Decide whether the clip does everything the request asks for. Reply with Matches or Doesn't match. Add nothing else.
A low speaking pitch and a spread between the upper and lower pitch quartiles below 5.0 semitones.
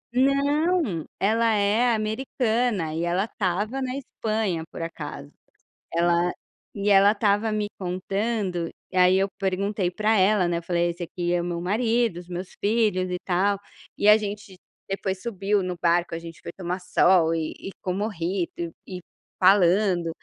Doesn't match